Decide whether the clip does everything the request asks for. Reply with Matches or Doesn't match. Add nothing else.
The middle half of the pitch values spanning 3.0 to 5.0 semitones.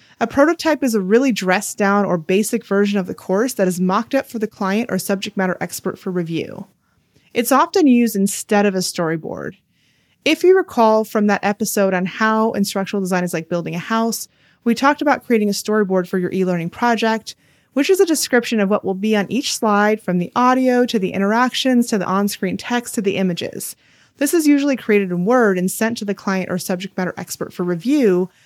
Matches